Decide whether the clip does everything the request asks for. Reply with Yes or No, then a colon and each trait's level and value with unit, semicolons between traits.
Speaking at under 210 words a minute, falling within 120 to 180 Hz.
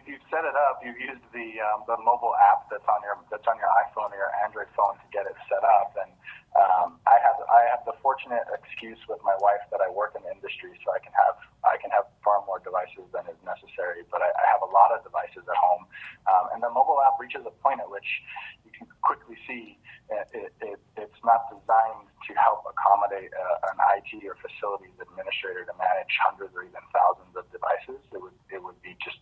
No: fast, 230 wpm; low, 135 Hz